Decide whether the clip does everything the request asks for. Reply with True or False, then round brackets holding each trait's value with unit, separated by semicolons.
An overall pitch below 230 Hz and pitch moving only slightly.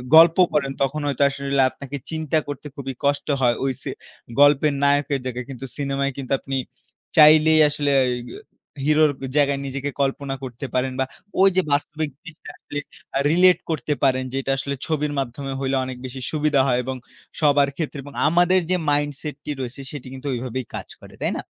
True (140 Hz; 2.0 semitones)